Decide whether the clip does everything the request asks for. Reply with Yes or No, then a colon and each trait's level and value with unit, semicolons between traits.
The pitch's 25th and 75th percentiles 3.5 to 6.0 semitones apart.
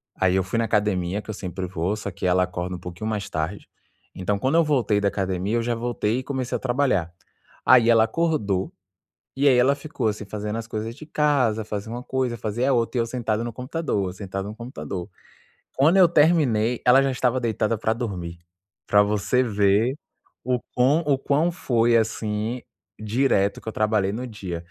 Yes: average, 4.1 semitones